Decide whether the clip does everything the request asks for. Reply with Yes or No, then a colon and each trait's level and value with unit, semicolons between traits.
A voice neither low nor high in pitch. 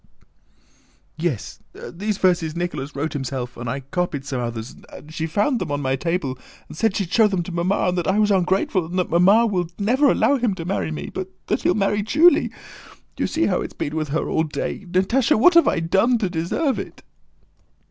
Yes: medium, 175 Hz